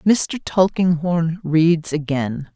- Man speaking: No, female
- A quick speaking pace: No, slow, 95 wpm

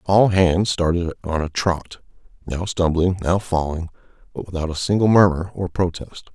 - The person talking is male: Yes, male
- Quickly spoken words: No, average, 160 wpm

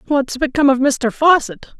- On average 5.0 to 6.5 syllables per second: Yes, 5.3 syllables/s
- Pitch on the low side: No, very high, 275 Hz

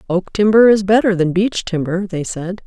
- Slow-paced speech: No, average, 200 wpm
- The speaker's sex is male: No, female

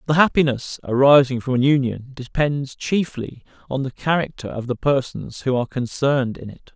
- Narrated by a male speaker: Yes, male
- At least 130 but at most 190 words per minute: Yes, average, 170 wpm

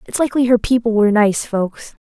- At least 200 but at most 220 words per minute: Yes, fast, 205 wpm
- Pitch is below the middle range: No, high, 225 Hz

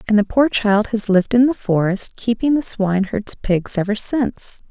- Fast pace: No, average, 190 wpm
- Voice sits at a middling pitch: No, high, 215 Hz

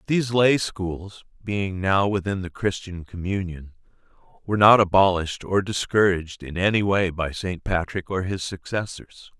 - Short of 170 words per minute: Yes, average, 145 wpm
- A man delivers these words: Yes, male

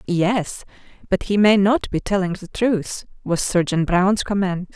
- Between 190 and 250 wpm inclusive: No, average, 165 wpm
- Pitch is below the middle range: No, high, 190 Hz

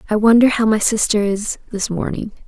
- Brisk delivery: No, average, 195 wpm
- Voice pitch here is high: Yes, high, 215 Hz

